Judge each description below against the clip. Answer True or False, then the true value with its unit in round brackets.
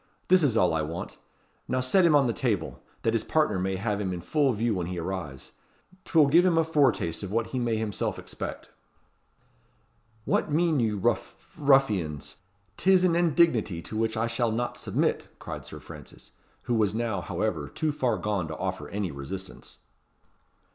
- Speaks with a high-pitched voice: False (115 Hz)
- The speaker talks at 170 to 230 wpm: True (180 wpm)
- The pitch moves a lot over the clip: True (6.9 semitones)